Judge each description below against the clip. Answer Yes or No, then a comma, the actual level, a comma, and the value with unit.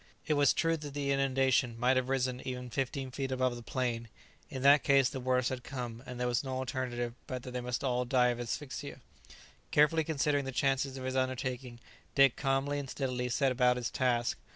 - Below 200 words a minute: No, fast, 205 wpm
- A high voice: No, low, 130 Hz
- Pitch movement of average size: No, narrow, 1.7 semitones